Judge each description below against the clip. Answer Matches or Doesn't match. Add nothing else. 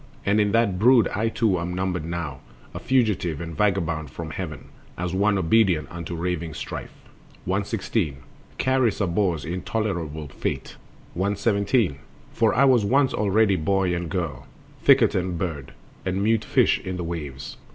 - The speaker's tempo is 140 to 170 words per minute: Matches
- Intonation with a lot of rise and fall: Doesn't match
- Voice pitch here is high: Doesn't match